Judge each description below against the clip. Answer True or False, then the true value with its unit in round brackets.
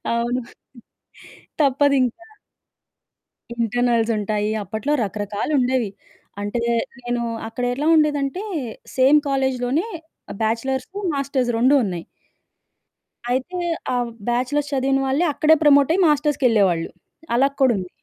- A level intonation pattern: False (3.6 semitones)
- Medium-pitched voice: False (255 Hz)